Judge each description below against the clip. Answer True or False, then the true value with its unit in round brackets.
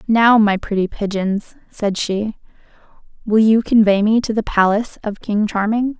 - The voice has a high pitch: True (215 Hz)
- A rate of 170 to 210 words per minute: False (160 wpm)